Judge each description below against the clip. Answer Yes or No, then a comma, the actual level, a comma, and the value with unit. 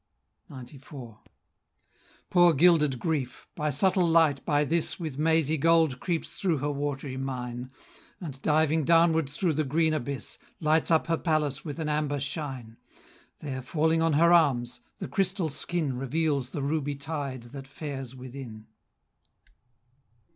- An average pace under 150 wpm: Yes, average, 140 wpm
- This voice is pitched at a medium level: Yes, medium, 150 Hz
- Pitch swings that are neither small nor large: Yes, average, 3.3 semitones